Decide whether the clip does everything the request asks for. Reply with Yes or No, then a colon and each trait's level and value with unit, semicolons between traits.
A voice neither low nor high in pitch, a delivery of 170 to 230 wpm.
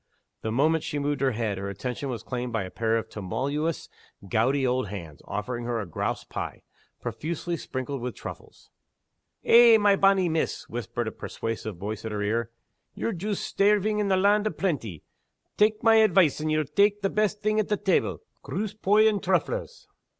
Yes: medium, 145 Hz; average, 180 wpm